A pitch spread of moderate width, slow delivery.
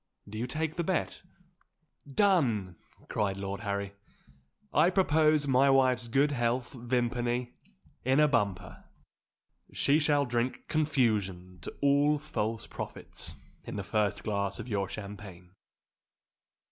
No: wide, 6.0 semitones; slow, 120 wpm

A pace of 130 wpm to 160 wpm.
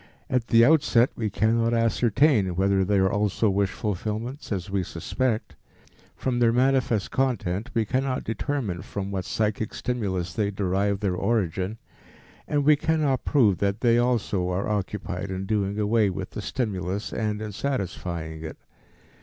Yes: average, 155 wpm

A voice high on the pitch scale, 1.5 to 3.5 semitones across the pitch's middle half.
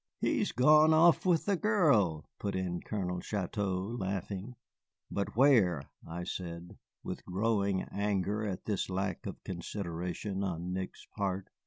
No: low, 100 Hz; average, 3.2 semitones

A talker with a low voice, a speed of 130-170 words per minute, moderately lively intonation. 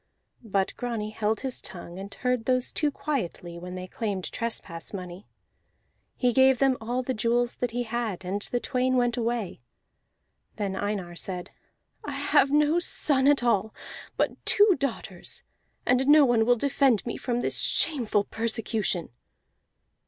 No: high, 235 Hz; average, 150 wpm; average, 4.2 semitones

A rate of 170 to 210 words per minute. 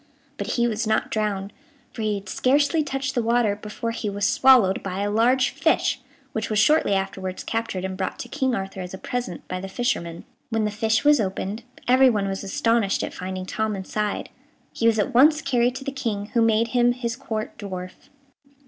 Yes: average, 200 wpm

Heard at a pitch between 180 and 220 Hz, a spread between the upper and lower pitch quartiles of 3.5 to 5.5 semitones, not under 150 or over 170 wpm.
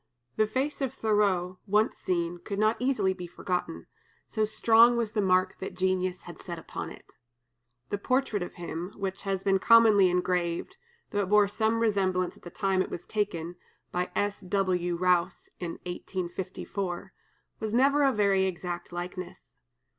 No: high, 190 Hz; average, 2.9 semitones; average, 160 wpm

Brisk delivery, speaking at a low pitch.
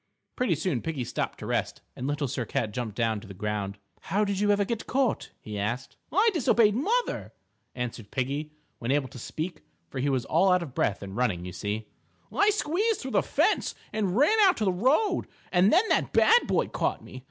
No: fast, 210 wpm; medium, 155 Hz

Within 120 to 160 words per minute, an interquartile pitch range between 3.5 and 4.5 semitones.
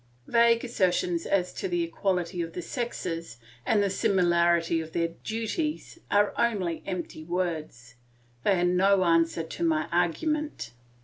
Yes: average, 140 wpm; average, 4.0 semitones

